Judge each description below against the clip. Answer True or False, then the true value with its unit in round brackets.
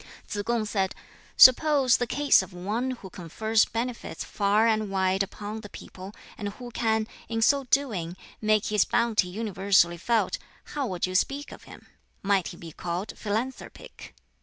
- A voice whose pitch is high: True (215 Hz)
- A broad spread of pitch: False (3.8 semitones)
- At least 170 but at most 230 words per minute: False (160 wpm)